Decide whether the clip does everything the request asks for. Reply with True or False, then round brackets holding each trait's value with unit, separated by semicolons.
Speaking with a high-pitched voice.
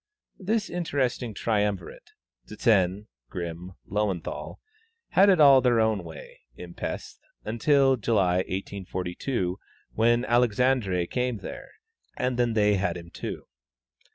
False (110 Hz)